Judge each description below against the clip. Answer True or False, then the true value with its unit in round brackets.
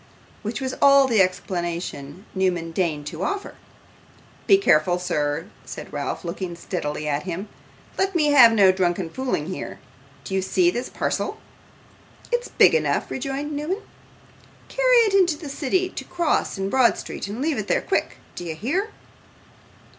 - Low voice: False (205 Hz)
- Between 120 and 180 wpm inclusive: True (160 wpm)